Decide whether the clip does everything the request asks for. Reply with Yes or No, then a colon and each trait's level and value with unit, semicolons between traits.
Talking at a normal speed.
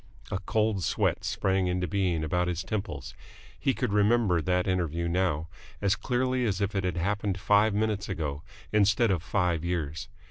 Yes: average, 170 wpm